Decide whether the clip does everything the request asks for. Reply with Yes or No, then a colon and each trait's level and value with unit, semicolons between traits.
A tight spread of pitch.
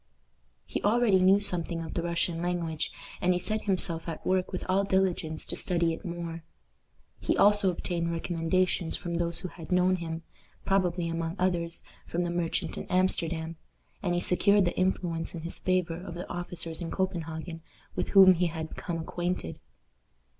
Yes: narrow, 1.9 semitones